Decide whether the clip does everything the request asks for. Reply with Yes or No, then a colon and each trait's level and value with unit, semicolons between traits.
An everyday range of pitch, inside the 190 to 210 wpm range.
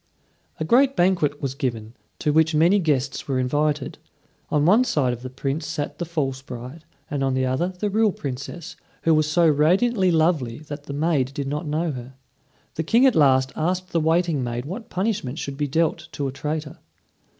Yes: average, 4.1 semitones; average, 195 wpm